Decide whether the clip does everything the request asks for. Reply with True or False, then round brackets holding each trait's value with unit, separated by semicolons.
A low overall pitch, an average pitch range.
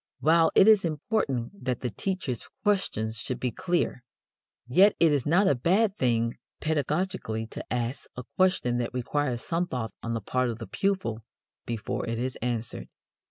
False (130 Hz; 7.1 semitones)